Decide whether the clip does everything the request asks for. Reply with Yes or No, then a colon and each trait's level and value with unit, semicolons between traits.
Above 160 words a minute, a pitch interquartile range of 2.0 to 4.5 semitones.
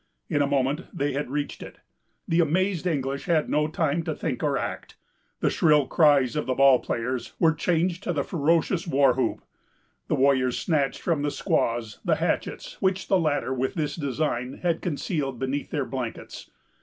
Yes: average, 180 wpm; average, 3.6 semitones